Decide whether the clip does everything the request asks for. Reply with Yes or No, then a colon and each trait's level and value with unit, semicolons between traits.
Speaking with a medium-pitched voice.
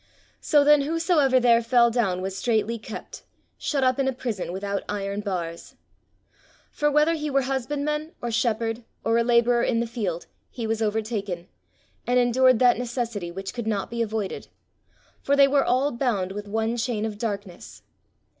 No: high, 235 Hz